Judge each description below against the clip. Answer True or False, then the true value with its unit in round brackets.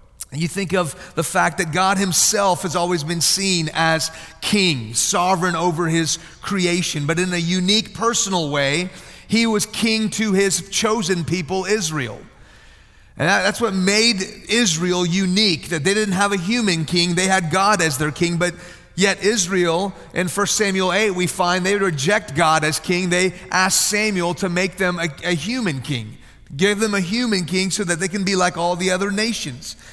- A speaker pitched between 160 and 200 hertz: True (185 Hz)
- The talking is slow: False (180 wpm)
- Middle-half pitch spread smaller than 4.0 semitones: True (2.7 semitones)